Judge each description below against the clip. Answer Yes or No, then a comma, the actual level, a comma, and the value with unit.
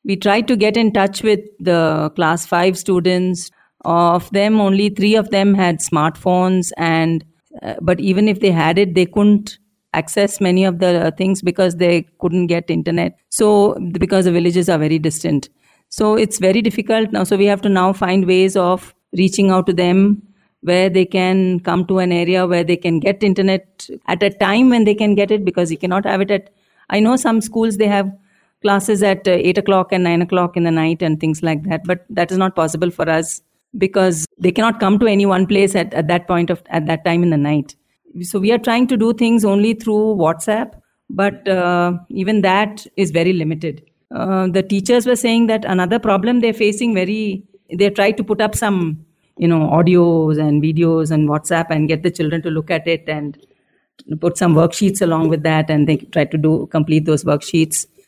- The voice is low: No, medium, 185 Hz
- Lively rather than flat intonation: No, average, 3.2 semitones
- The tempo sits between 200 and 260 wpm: Yes, fast, 205 wpm